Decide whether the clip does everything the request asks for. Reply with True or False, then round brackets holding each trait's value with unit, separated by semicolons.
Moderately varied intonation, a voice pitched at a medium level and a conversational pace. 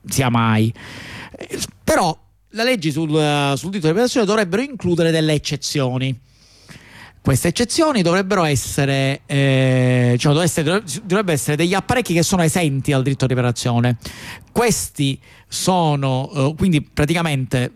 True (5.0 semitones; 145 Hz; 135 wpm)